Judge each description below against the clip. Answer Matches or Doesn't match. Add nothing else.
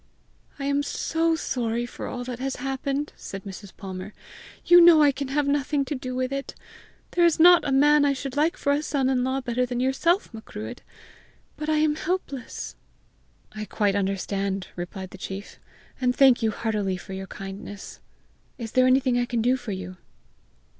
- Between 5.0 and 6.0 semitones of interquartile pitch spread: Matches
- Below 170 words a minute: Doesn't match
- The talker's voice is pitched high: Matches